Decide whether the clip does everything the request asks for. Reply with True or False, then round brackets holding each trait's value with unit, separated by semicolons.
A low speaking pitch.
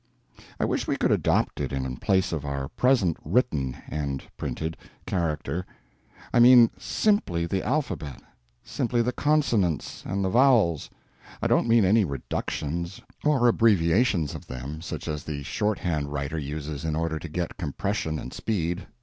True (85 Hz)